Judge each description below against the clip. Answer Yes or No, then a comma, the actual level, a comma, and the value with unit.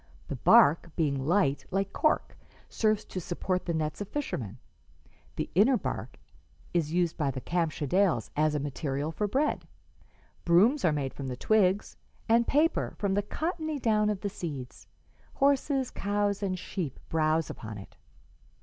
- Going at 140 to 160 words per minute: Yes, average, 155 wpm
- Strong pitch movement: Yes, wide, 5.8 semitones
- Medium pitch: Yes, medium, 180 Hz